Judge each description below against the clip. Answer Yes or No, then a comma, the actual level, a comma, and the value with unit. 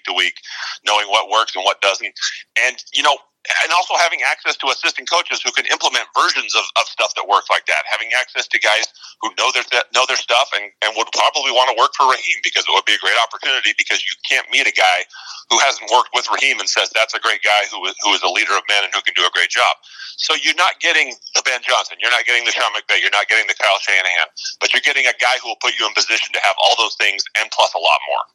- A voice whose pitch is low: Yes, low, 115 Hz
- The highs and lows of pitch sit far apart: Yes, wide, 7.1 semitones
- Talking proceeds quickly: Yes, fast, 270 wpm